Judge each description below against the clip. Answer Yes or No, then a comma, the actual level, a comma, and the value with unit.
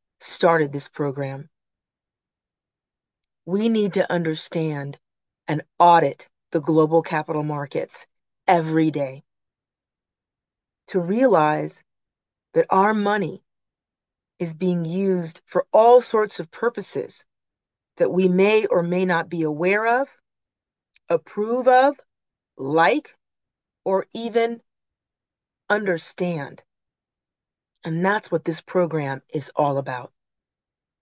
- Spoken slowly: Yes, slow, 100 wpm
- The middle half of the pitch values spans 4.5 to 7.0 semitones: Yes, average, 4.9 semitones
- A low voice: No, medium, 175 Hz